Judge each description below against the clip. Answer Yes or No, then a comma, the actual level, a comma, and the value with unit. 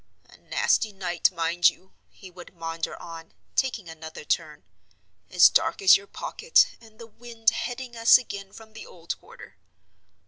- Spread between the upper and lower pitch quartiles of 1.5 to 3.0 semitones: No, average, 5.2 semitones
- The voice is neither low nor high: No, high, 195 Hz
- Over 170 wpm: No, average, 160 wpm